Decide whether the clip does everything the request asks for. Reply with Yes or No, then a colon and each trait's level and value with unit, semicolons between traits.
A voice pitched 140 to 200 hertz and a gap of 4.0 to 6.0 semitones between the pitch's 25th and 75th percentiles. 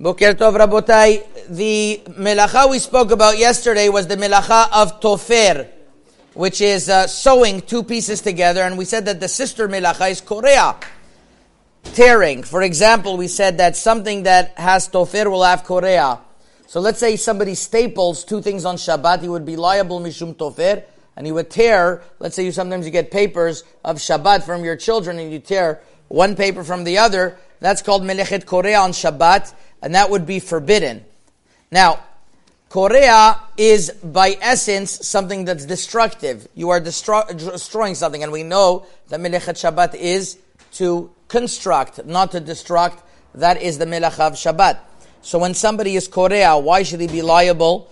No: medium, 185 Hz; average, 3.4 semitones